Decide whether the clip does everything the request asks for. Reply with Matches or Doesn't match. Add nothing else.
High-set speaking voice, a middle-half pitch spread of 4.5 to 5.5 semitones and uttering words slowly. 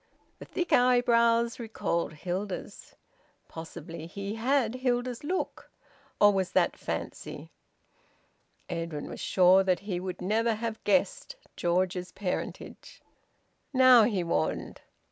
Matches